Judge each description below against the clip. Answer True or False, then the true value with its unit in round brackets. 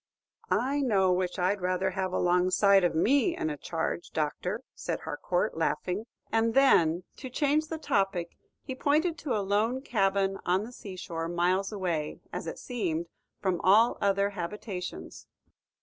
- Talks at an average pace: True (160 wpm)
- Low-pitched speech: False (195 Hz)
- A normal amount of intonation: True (4.7 semitones)